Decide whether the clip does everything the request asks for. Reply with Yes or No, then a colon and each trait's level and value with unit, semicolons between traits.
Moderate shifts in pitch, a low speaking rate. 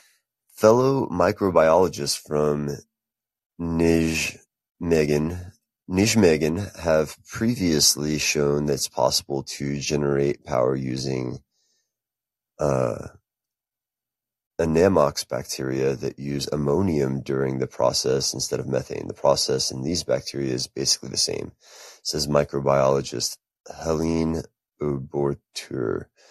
Yes: average, 4.7 semitones; slow, 95 wpm